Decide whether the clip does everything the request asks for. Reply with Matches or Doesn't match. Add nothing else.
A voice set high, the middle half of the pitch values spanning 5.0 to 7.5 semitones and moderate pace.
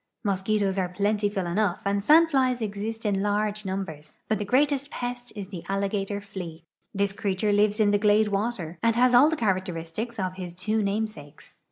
Doesn't match